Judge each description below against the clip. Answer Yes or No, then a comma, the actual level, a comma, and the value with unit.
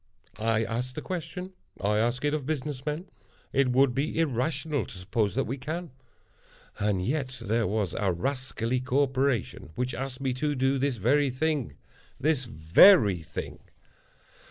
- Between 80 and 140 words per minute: No, average, 150 wpm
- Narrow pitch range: No, average, 4.3 semitones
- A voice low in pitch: Yes, low, 130 Hz